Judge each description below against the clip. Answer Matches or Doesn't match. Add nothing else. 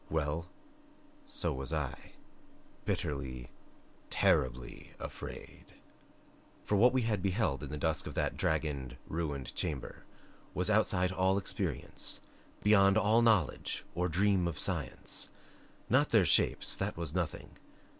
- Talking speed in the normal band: Doesn't match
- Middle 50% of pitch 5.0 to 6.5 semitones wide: Matches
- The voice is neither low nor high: Doesn't match